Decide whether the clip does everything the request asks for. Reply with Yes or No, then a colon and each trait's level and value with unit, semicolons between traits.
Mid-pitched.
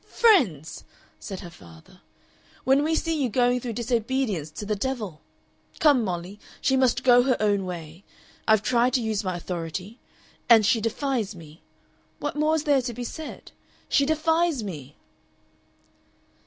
No: high, 230 Hz